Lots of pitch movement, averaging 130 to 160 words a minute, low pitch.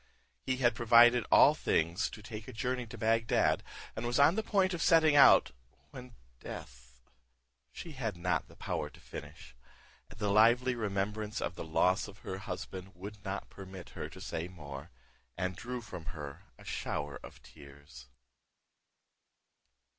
Yes: wide, 5.8 semitones; average, 155 wpm; low, 105 Hz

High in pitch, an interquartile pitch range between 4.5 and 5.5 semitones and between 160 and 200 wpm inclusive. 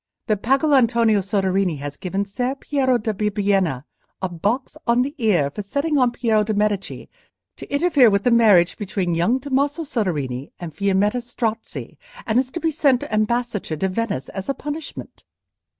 Yes: high, 215 Hz; average, 4.8 semitones; average, 165 wpm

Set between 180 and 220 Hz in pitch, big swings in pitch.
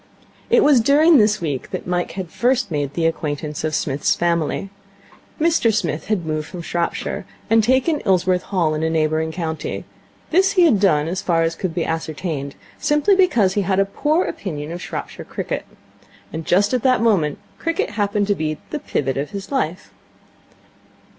Yes: medium, 185 Hz; wide, 6.3 semitones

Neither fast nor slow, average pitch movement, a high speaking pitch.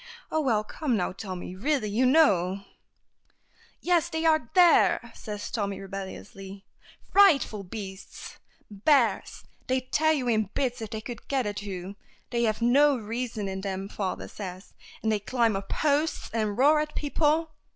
No: average, 160 wpm; wide, 6.3 semitones; high, 225 Hz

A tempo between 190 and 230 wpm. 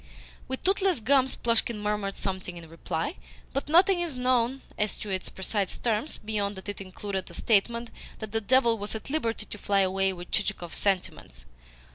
No: average, 175 wpm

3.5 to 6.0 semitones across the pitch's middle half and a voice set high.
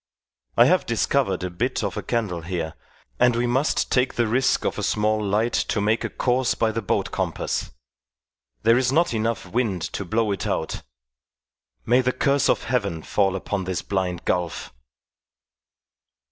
No: average, 4.6 semitones; low, 110 Hz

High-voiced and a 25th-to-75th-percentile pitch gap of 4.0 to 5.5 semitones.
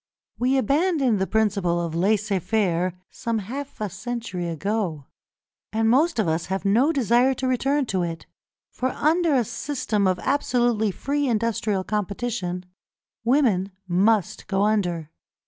Yes: high, 215 Hz; average, 5.2 semitones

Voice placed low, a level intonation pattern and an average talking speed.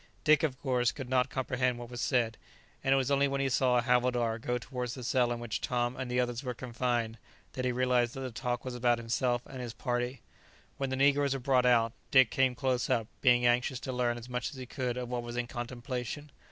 No: low, 125 Hz; narrow, 1.4 semitones; fast, 240 wpm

